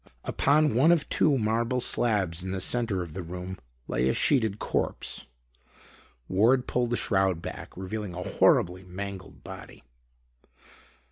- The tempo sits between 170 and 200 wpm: No, average, 140 wpm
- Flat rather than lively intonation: No, average, 4.8 semitones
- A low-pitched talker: Yes, low, 100 Hz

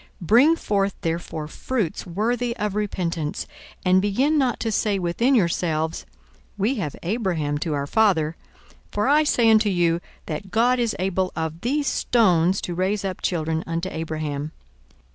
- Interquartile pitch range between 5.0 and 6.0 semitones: Yes, wide, 5.4 semitones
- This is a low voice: No, high, 190 Hz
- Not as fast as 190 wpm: Yes, average, 155 wpm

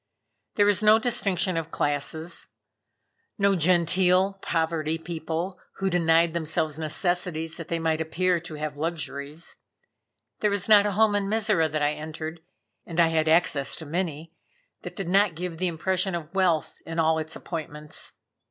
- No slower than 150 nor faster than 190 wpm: Yes, average, 160 wpm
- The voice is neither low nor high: Yes, medium, 165 Hz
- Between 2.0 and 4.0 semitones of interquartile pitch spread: Yes, average, 2.9 semitones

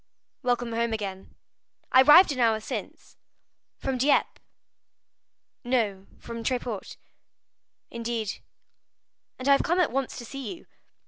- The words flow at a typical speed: No, slow, 125 wpm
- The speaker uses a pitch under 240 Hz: No, high, 245 Hz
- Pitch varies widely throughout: No, average, 3.1 semitones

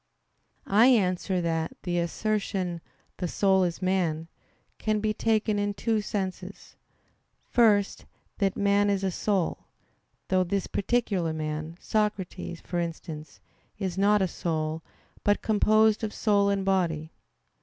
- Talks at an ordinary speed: No, slow, 130 wpm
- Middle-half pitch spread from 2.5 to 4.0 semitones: Yes, average, 3.3 semitones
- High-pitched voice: Yes, high, 195 Hz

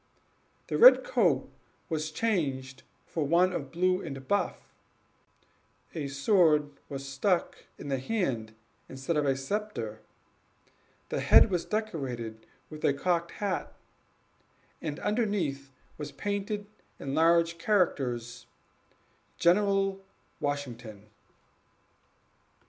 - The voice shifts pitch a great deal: Yes, wide, 5.9 semitones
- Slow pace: Yes, slow, 105 wpm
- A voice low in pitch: No, medium, 155 Hz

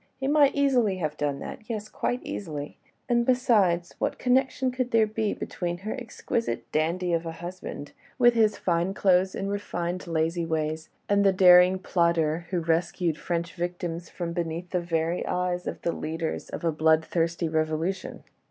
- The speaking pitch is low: No, medium, 175 Hz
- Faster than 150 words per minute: Yes, average, 165 wpm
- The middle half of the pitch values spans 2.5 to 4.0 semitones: Yes, average, 3.6 semitones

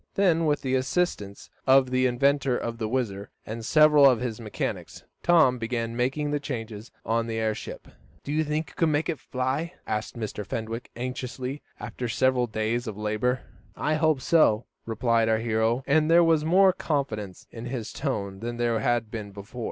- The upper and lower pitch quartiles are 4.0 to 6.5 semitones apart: Yes, average, 4.4 semitones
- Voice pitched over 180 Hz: No, low, 125 Hz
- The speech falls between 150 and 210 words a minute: Yes, average, 180 wpm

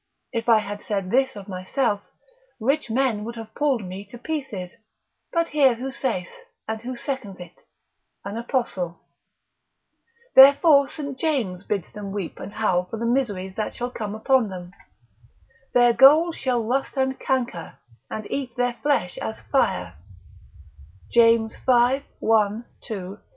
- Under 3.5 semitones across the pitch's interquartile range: No, average, 4.7 semitones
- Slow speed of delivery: No, average, 150 wpm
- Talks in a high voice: Yes, high, 230 Hz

